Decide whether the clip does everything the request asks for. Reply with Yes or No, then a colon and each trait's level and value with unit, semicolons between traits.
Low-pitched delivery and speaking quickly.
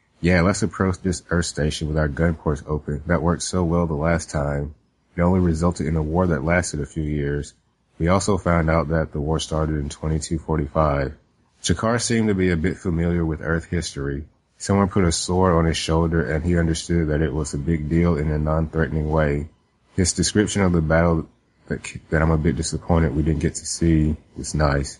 Yes: very low, 80 Hz; fast, 210 wpm